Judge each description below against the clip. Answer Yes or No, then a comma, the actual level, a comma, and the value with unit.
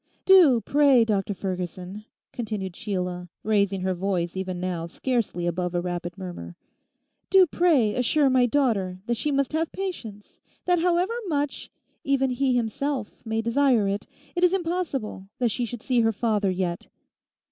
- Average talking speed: Yes, average, 150 wpm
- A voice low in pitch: No, high, 225 Hz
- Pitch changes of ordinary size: No, wide, 6.8 semitones